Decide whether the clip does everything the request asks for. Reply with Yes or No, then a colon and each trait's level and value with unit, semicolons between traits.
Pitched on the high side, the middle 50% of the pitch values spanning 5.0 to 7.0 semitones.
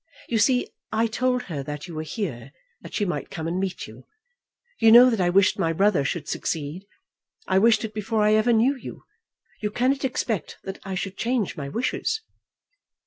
Yes: high, 205 Hz; wide, 5.6 semitones